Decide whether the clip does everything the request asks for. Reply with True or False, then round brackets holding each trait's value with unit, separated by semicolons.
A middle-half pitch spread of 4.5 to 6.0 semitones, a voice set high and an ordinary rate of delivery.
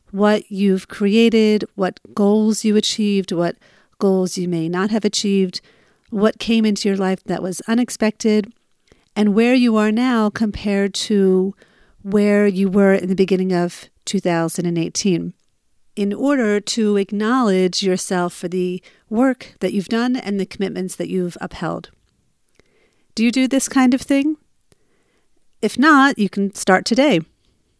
False (2.9 semitones; 200 Hz; 145 wpm)